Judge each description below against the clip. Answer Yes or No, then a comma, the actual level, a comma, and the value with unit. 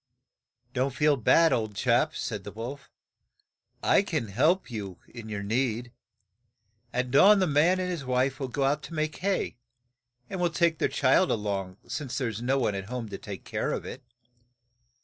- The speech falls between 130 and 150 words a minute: No, average, 190 wpm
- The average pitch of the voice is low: Yes, low, 130 Hz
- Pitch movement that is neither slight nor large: No, wide, 5.7 semitones